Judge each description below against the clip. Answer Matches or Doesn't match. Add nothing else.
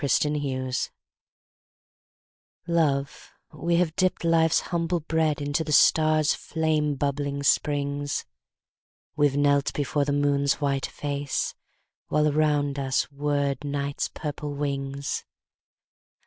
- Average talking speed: Doesn't match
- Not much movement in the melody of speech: Matches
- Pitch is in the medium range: Matches